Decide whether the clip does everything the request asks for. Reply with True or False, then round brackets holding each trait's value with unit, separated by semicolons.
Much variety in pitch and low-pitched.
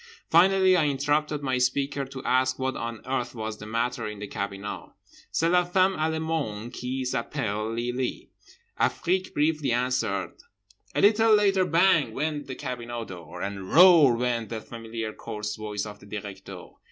True (6.0 semitones; 125 Hz)